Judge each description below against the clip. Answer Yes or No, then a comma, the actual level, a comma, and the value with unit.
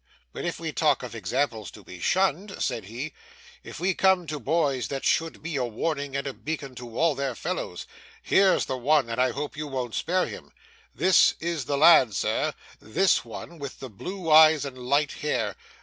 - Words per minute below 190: No, average, 195 wpm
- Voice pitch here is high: No, medium, 145 Hz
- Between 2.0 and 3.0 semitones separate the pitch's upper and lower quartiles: No, average, 4.5 semitones